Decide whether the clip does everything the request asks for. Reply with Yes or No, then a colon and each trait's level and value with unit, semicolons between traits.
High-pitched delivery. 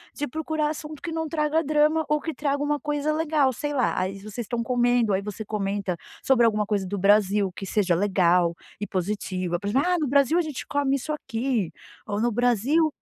Yes: high, 245 Hz